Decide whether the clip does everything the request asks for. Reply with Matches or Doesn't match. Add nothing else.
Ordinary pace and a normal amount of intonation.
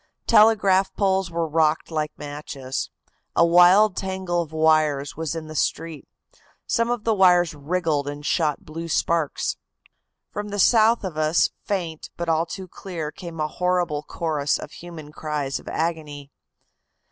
Matches